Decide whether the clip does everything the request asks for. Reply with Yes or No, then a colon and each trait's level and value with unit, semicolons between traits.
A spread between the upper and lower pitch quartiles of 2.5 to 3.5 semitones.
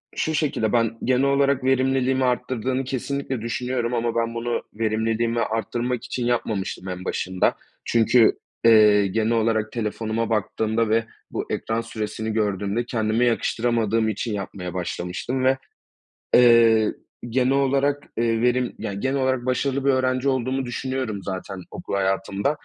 Yes: average, 2.8 semitones